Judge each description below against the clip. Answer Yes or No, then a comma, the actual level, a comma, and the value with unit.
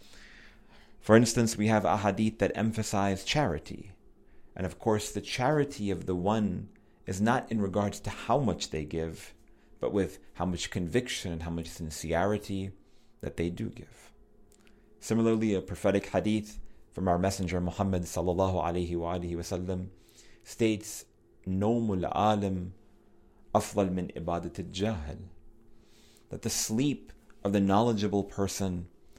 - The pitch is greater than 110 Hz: No, low, 100 Hz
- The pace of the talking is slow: Yes, slow, 120 wpm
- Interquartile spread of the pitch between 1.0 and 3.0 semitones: No, average, 3.4 semitones